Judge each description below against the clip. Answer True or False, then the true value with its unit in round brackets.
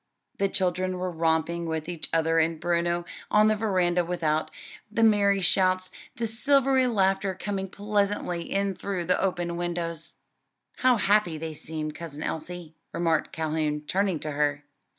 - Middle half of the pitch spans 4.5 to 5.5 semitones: False (3.4 semitones)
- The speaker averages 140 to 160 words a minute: True (150 wpm)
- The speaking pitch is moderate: True (175 Hz)